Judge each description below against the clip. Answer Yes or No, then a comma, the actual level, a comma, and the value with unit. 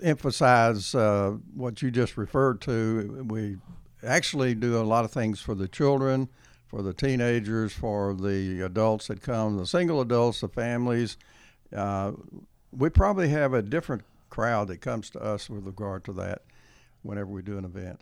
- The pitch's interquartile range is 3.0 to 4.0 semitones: Yes, average, 3.6 semitones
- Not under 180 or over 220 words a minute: No, average, 165 wpm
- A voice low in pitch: Yes, low, 110 Hz